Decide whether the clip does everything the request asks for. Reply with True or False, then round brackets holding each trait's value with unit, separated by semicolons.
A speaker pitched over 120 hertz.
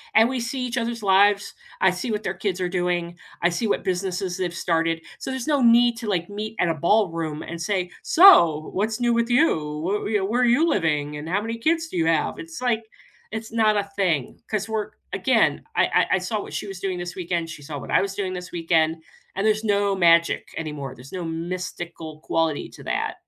True (190 Hz)